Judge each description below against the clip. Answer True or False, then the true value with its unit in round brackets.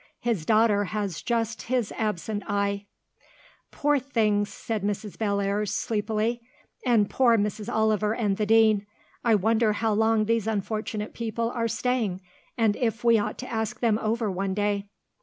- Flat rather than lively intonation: True (1.9 semitones)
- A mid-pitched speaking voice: False (215 Hz)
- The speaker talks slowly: False (155 wpm)